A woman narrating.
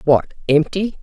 Yes: female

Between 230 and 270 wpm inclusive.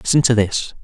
No: fast, 215 wpm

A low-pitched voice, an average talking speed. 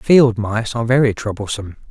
Yes: low, 115 Hz; average, 160 wpm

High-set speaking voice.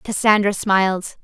Yes: high, 200 Hz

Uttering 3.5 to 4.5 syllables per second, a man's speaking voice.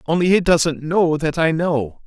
Yes: 4.1 syllables/s; male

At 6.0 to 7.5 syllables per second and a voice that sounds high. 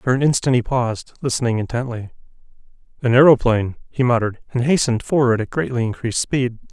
No: 6.5 syllables/s; low, 125 Hz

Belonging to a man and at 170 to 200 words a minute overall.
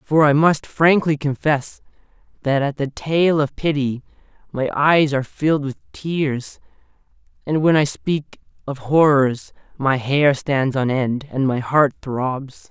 No: male; average, 150 wpm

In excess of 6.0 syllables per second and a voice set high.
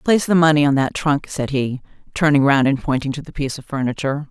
No: 6.4 syllables/s; medium, 140 Hz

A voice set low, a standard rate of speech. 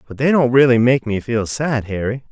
No: low, 125 Hz; fast, 235 wpm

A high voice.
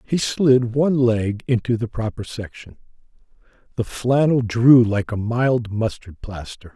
No: low, 115 Hz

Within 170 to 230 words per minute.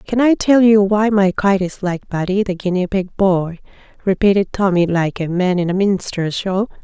Yes: average, 200 wpm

